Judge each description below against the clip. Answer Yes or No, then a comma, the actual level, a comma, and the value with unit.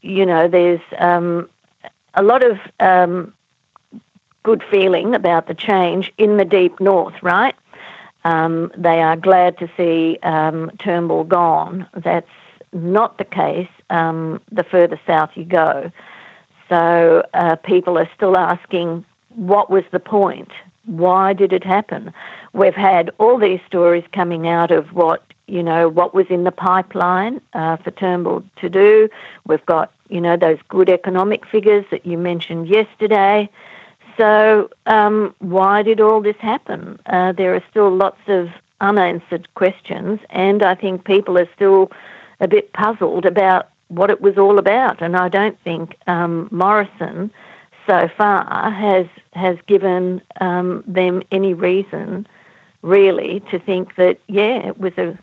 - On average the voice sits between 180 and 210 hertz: Yes, medium, 185 Hz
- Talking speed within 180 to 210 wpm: No, average, 150 wpm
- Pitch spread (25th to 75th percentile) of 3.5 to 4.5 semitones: No, narrow, 2.5 semitones